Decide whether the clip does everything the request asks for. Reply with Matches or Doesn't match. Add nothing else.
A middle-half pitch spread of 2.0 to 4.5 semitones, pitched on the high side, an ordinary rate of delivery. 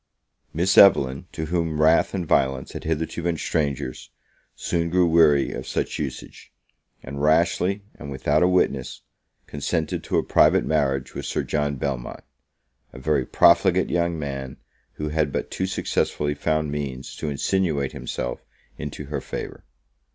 Doesn't match